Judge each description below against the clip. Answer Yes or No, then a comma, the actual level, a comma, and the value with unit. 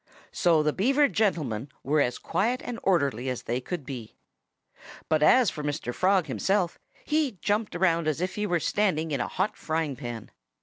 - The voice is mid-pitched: Yes, medium, 165 Hz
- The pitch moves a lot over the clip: Yes, wide, 5.8 semitones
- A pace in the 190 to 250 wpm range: No, average, 180 wpm